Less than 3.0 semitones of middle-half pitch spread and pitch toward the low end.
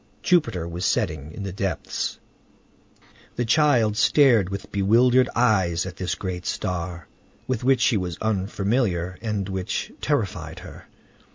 No: average, 4.7 semitones; low, 100 Hz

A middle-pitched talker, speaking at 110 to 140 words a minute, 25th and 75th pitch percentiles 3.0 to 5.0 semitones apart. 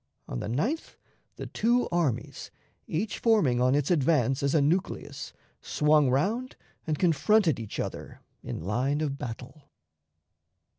No: medium, 150 Hz; slow, 135 wpm; wide, 5.6 semitones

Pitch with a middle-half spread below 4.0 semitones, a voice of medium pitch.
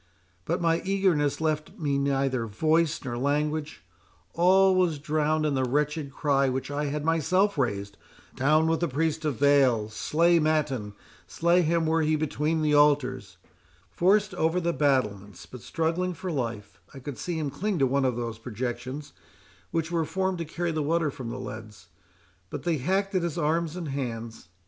No: average, 4.3 semitones; medium, 150 Hz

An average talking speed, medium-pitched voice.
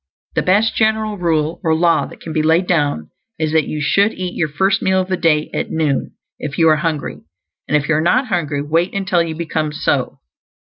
No: fast, 215 wpm; medium, 165 Hz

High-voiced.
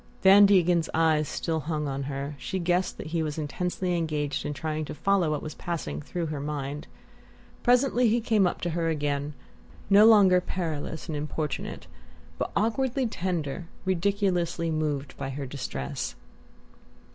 No: medium, 165 Hz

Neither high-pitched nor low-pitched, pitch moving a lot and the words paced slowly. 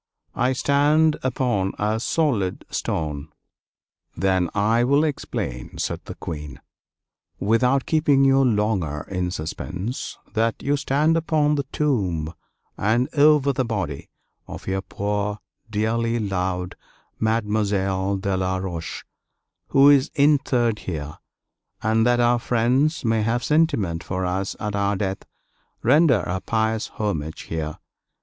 No: low, 110 Hz; wide, 6.0 semitones; slow, 125 wpm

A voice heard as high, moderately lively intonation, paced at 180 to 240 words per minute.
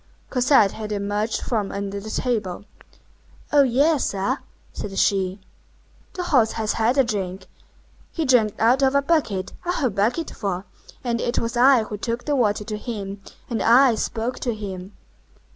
No: high, 225 Hz; average, 4.1 semitones; average, 160 wpm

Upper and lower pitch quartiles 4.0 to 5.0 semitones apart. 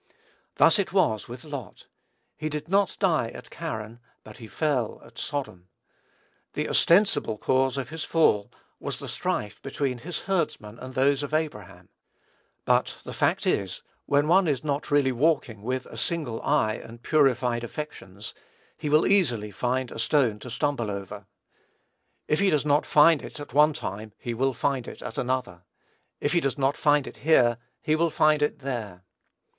Yes: average, 4.6 semitones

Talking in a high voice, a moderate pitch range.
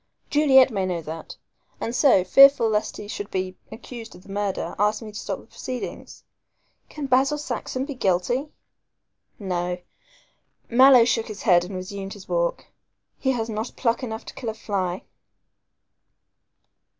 Yes: high, 220 Hz; average, 5.0 semitones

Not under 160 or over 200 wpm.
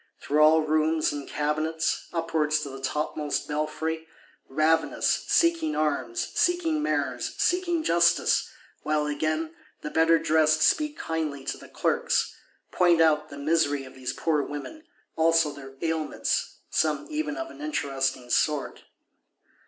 No: slow, 135 wpm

